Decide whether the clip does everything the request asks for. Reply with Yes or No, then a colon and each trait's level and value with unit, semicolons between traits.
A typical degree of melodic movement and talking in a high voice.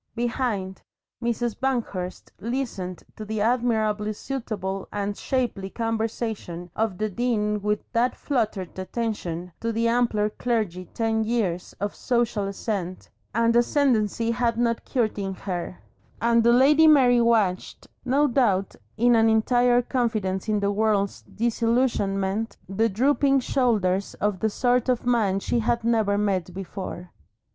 Yes: average, 3.3 semitones; high, 220 Hz